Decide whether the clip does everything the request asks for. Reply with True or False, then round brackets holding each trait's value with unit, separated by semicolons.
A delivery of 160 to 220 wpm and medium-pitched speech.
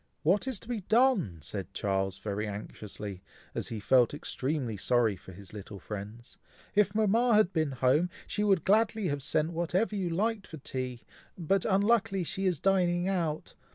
True (175 wpm; 160 Hz)